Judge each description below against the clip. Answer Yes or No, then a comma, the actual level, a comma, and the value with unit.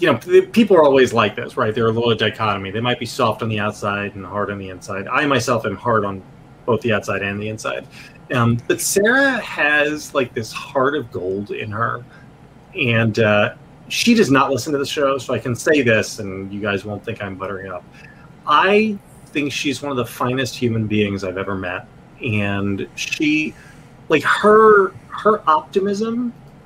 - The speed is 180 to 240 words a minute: Yes, average, 195 wpm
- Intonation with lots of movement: Yes, wide, 6.3 semitones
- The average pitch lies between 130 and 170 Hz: No, low, 120 Hz